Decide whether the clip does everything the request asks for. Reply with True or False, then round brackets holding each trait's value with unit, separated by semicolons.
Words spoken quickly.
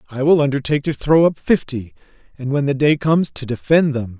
True (215 wpm)